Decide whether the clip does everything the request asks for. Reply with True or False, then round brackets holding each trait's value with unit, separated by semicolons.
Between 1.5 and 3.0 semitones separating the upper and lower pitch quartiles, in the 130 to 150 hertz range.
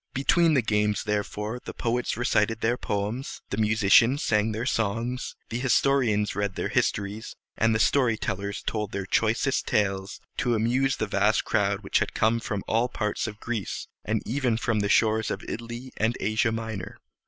False (2.4 semitones; 110 Hz)